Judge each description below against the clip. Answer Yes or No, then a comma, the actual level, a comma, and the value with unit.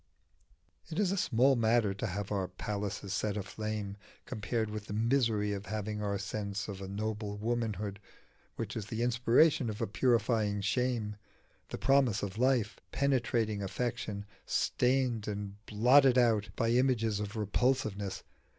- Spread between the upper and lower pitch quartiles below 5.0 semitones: Yes, average, 2.8 semitones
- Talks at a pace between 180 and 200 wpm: No, average, 150 wpm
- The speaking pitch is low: Yes, low, 110 Hz